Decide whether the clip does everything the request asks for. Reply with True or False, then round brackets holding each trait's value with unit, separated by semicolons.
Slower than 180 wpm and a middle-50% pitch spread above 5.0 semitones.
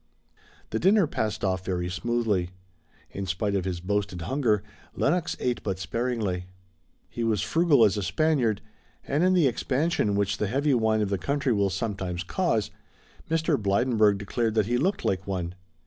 True (165 wpm; 5.4 semitones)